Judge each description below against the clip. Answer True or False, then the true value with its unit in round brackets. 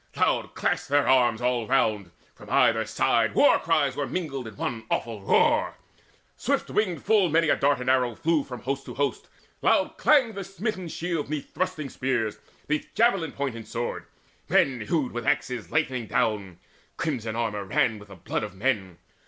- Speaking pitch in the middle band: False (130 Hz)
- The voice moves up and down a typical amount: False (5.8 semitones)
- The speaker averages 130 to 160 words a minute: False (180 wpm)